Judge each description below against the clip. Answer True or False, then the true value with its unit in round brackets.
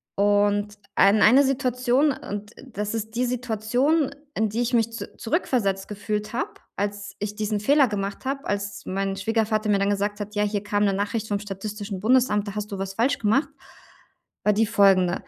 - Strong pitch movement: False (2.7 semitones)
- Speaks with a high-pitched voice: True (210 Hz)